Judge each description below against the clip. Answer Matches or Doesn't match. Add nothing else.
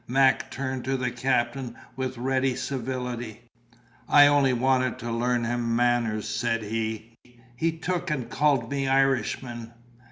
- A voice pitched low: Matches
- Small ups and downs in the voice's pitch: Matches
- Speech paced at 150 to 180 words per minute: Doesn't match